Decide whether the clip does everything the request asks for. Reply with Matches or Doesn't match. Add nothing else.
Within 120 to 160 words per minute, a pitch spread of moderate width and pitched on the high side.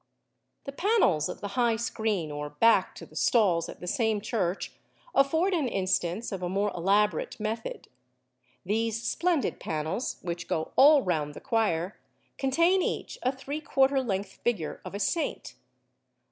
Doesn't match